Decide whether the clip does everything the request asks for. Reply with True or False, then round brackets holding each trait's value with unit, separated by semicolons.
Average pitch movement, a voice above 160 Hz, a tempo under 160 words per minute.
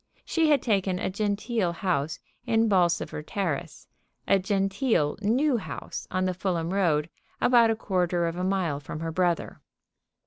True (3.7 semitones; 185 Hz; 150 wpm)